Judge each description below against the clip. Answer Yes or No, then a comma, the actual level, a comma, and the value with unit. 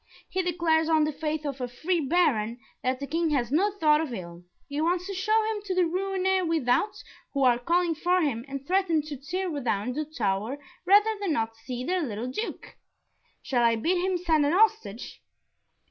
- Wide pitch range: Yes, wide, 6.3 semitones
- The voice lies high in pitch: Yes, very high, 310 Hz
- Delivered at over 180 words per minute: Yes, average, 195 wpm